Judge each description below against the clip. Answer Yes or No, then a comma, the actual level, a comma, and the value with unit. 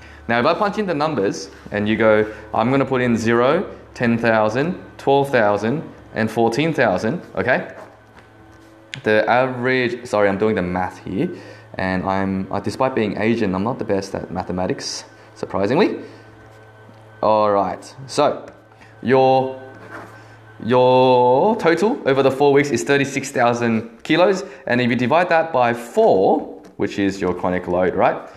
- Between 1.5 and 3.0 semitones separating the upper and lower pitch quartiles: No, average, 3.4 semitones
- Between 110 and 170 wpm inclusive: Yes, average, 140 wpm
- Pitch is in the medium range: No, low, 110 Hz